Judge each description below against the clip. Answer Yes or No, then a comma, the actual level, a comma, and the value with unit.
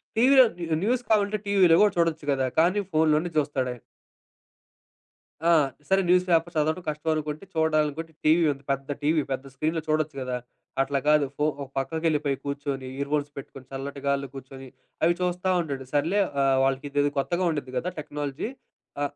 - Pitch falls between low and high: Yes, medium, 150 Hz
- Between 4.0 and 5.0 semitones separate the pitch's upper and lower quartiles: No, average, 3.4 semitones